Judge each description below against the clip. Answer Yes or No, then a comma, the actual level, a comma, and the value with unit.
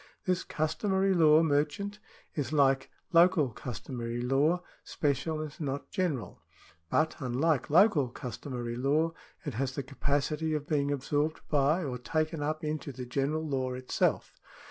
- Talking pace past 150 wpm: No, average, 140 wpm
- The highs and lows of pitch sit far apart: No, average, 3.1 semitones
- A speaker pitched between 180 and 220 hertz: No, medium, 145 Hz